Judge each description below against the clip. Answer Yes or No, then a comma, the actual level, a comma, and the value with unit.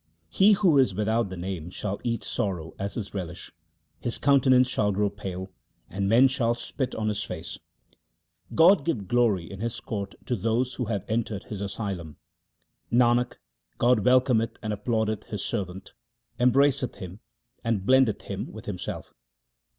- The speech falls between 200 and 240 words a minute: No, average, 160 wpm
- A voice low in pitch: Yes, low, 110 Hz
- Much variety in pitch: No, average, 4.0 semitones